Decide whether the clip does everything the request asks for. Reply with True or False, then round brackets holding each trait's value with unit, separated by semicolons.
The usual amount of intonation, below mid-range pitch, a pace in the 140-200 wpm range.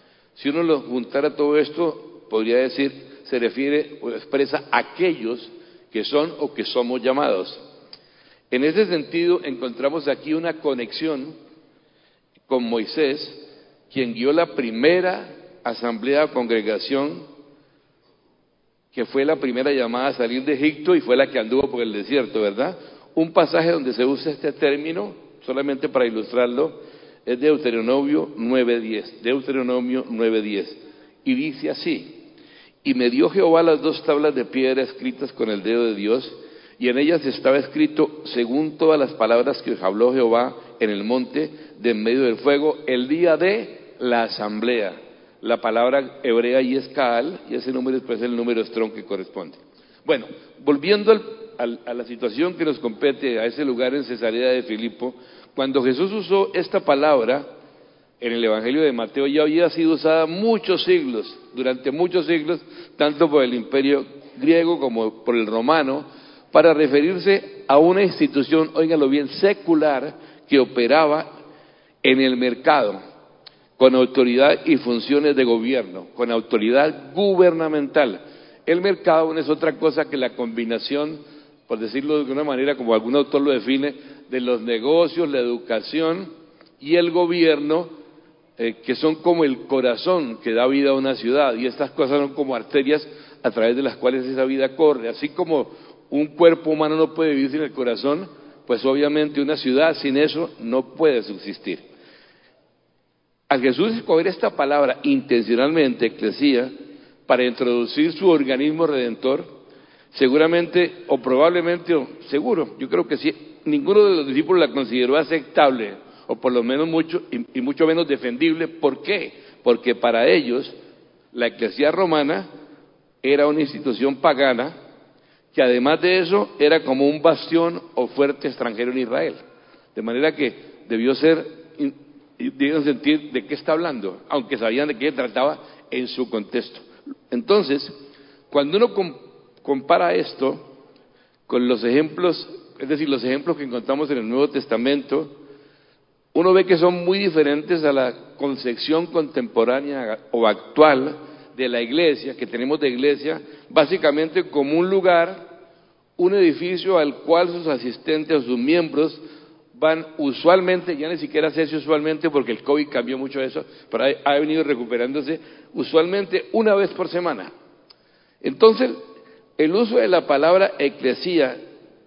False (4.1 semitones; 145 Hz; 150 wpm)